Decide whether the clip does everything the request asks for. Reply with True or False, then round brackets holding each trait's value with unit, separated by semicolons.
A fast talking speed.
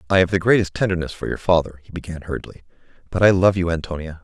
True (225 wpm)